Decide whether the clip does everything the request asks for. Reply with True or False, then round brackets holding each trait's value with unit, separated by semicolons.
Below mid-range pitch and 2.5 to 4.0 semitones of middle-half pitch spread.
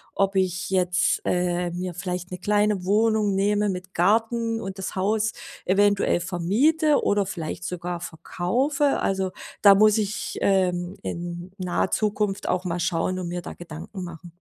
False (190 Hz; 2.8 semitones)